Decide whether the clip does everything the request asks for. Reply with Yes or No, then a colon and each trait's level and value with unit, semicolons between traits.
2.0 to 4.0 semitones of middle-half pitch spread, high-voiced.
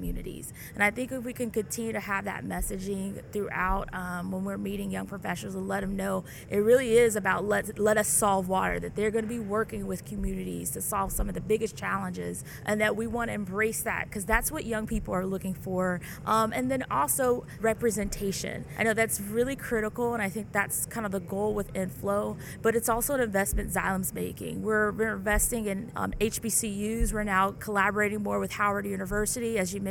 Yes: narrow, 2.5 semitones; high, 205 Hz